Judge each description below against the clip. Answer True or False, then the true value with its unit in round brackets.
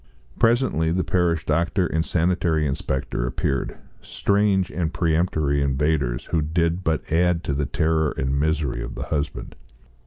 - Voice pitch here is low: True (80 Hz)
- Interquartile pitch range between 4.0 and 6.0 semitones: False (3.2 semitones)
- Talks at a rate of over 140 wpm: False (135 wpm)